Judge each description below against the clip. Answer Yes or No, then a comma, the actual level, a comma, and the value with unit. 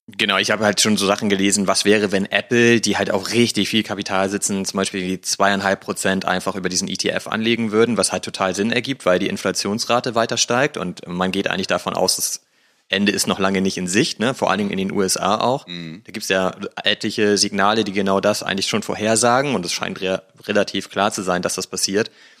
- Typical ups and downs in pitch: No, narrow, 2.2 semitones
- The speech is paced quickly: Yes, fast, 230 wpm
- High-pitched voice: No, low, 100 Hz